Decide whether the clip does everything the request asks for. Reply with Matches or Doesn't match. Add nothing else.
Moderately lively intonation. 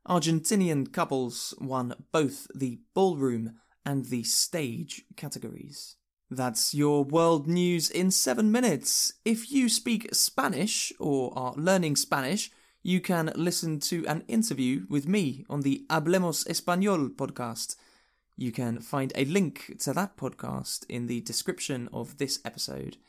Doesn't match